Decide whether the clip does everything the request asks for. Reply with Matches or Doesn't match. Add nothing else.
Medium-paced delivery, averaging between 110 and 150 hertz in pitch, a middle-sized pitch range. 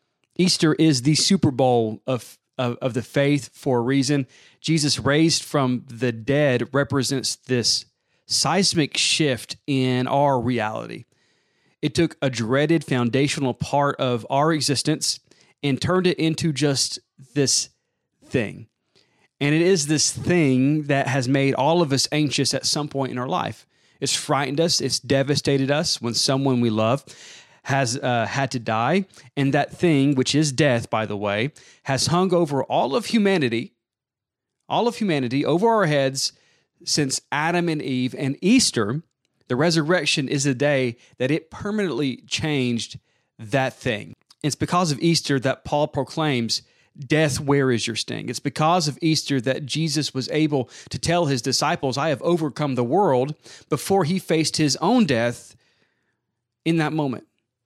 Matches